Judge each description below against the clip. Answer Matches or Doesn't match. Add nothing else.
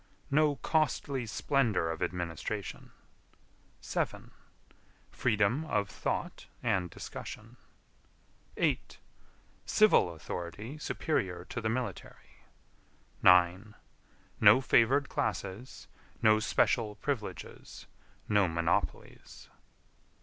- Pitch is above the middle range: Doesn't match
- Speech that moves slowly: Matches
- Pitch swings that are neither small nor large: Doesn't match